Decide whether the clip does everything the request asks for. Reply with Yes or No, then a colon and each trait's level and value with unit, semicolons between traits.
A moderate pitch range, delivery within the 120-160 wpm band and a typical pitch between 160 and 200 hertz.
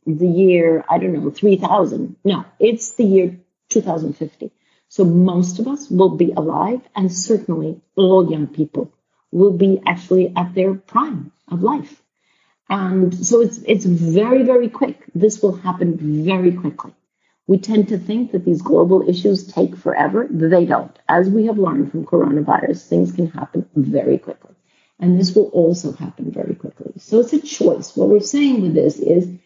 No: average, 3.5 semitones; average, 175 wpm; medium, 185 Hz